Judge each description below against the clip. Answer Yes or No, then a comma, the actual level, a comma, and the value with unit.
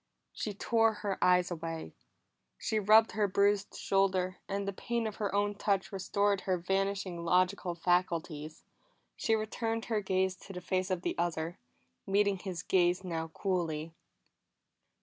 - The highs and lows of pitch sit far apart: No, narrow, 2.4 semitones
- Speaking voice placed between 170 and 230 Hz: Yes, high, 190 Hz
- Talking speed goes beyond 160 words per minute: No, average, 150 wpm